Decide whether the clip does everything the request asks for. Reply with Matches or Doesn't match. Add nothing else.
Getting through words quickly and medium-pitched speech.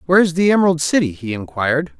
Matches